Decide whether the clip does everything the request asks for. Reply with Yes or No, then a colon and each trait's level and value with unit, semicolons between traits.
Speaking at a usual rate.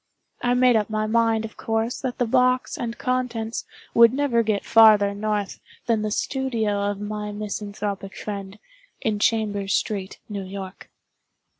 Yes: average, 150 wpm